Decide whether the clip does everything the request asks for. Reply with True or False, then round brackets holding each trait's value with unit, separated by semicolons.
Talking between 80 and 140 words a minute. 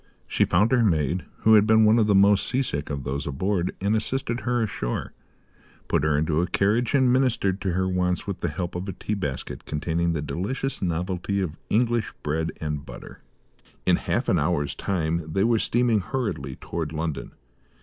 False (190 wpm)